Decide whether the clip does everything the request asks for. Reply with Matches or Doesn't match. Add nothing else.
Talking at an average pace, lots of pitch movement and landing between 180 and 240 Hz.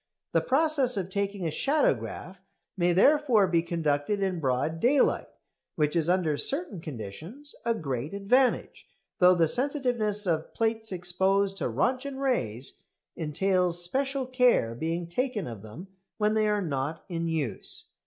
Matches